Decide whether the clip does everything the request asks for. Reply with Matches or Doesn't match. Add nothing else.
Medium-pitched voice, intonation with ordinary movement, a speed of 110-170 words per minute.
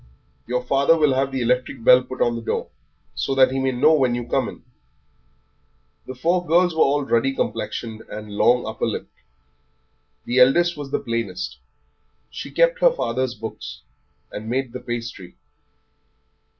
Doesn't match